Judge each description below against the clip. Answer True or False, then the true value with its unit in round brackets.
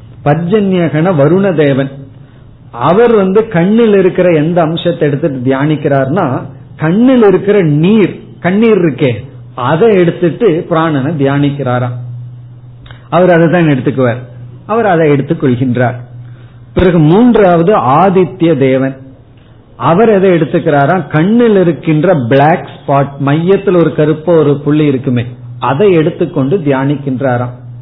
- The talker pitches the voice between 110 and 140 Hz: False (150 Hz)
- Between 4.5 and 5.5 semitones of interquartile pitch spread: True (5.1 semitones)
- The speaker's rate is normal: True (100 wpm)